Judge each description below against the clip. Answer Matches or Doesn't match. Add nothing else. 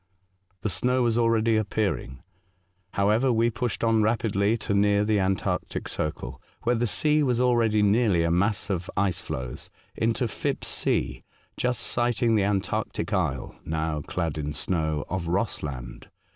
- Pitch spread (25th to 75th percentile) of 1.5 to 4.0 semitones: Doesn't match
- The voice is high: Doesn't match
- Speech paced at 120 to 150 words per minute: Matches